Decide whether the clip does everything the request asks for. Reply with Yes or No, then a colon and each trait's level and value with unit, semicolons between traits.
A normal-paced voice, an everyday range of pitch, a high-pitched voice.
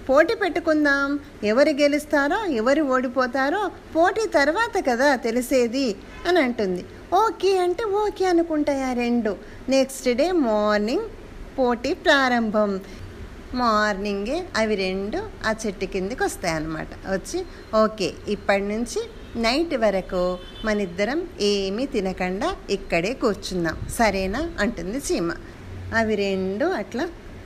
No: average, 100 wpm; wide, 7.4 semitones; very high, 255 Hz